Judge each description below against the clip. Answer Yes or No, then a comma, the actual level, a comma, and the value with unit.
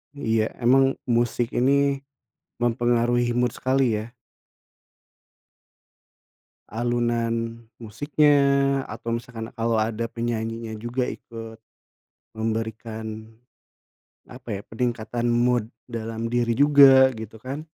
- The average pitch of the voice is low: Yes, low, 120 Hz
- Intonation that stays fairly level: Yes, narrow, 1.8 semitones